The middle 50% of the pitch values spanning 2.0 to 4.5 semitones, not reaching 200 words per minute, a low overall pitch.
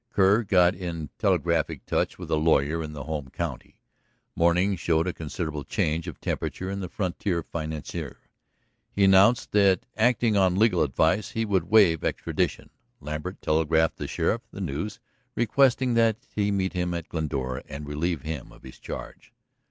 Yes: average, 4.2 semitones; average, 160 wpm; very low, 85 Hz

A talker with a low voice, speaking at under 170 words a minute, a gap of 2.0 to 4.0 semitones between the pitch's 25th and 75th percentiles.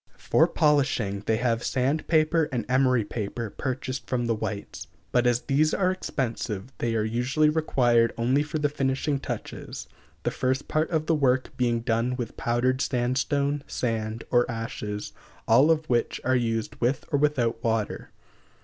Yes: low, 125 Hz; average, 160 wpm; average, 3.7 semitones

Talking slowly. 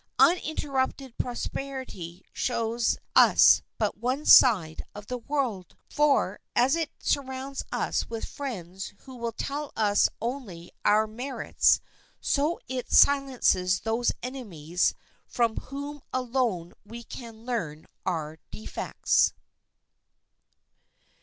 Yes: slow, 105 wpm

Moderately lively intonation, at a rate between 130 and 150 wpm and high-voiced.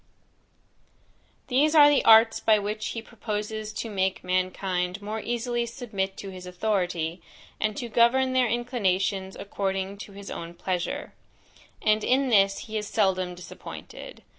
Yes: average, 3.6 semitones; average, 140 wpm; high, 210 Hz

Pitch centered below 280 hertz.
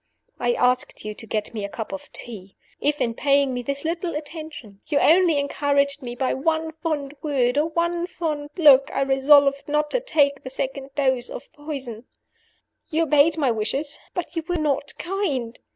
No: very high, 285 Hz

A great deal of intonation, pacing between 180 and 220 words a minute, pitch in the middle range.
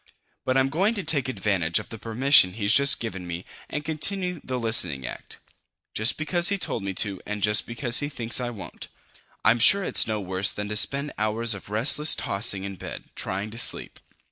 No: wide, 5.8 semitones; average, 200 wpm; low, 115 Hz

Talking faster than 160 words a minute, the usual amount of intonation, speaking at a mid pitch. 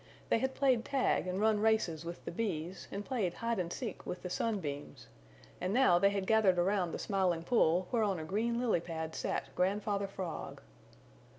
No: average, 195 wpm; average, 4.1 semitones; high, 195 Hz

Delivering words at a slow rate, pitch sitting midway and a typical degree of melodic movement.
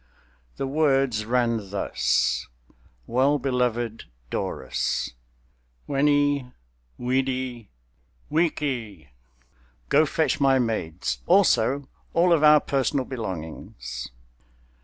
No: slow, 80 wpm; low, 130 Hz; average, 4.5 semitones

